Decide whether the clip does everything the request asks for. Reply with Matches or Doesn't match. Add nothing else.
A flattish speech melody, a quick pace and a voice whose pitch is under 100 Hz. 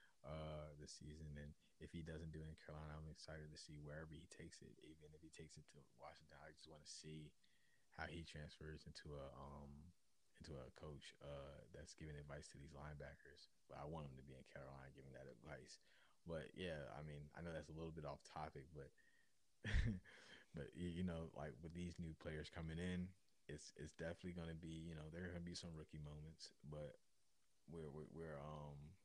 Matches